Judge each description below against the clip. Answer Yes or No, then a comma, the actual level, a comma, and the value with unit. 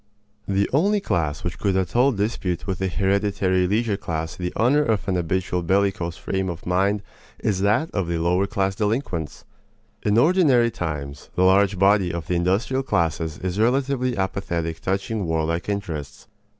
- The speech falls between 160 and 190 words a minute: Yes, average, 165 wpm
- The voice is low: Yes, very low, 95 Hz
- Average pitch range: Yes, average, 3.5 semitones